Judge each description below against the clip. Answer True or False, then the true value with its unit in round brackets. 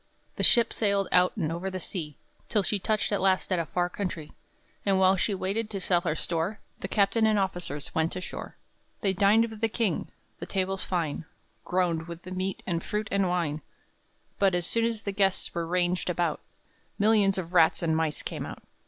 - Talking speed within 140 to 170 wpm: False (200 wpm)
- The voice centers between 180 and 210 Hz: True (185 Hz)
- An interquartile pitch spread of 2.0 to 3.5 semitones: True (2.8 semitones)